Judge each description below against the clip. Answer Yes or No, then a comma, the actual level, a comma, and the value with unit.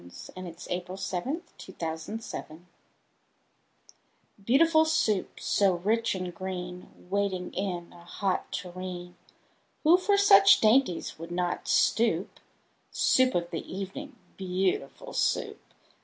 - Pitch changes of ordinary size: Yes, average, 4.1 semitones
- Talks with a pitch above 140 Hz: Yes, high, 190 Hz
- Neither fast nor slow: No, slow, 110 wpm